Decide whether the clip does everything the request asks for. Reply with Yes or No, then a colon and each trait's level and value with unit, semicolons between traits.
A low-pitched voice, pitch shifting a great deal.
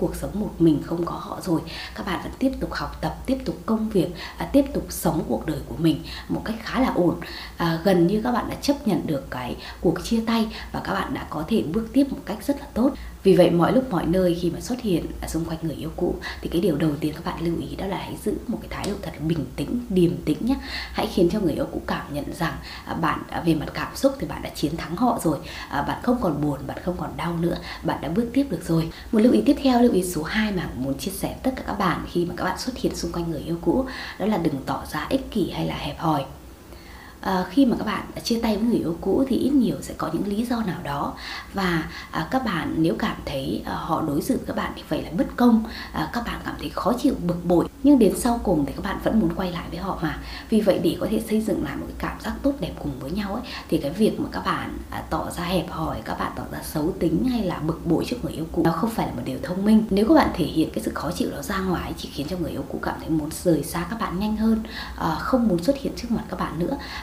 No: medium, 185 Hz; wide, 6.0 semitones